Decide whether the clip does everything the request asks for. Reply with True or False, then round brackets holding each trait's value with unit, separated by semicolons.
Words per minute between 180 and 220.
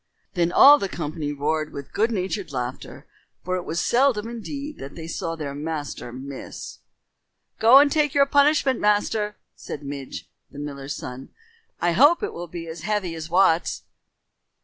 False (165 wpm)